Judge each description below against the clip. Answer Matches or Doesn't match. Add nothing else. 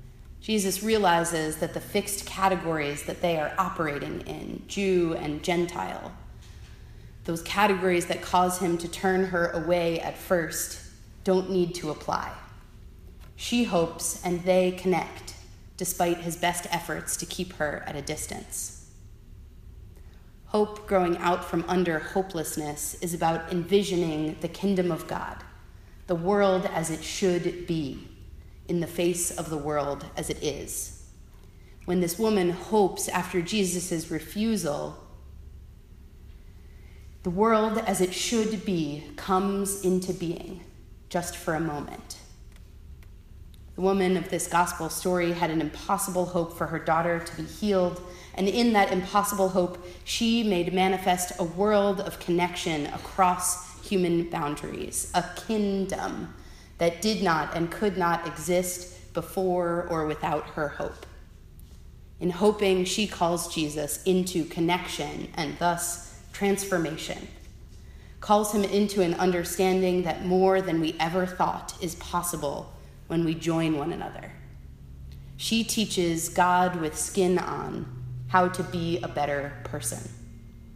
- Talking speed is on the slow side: Matches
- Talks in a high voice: Doesn't match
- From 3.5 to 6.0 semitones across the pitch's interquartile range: Doesn't match